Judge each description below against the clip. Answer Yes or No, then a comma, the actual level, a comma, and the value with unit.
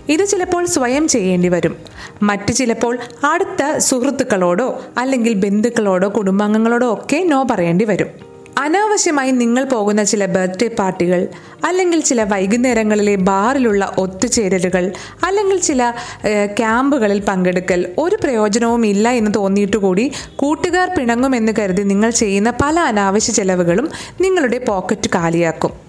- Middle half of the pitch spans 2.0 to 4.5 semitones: No, average, 5.2 semitones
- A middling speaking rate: Yes, average, 110 wpm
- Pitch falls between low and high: No, high, 230 Hz